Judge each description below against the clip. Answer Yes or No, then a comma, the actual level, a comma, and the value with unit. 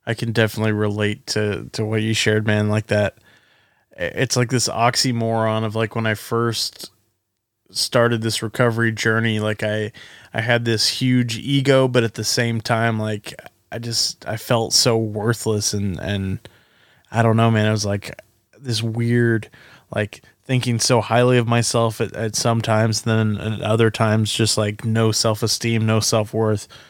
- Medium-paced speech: Yes, average, 165 wpm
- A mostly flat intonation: Yes, narrow, 1.5 semitones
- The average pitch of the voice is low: Yes, low, 115 Hz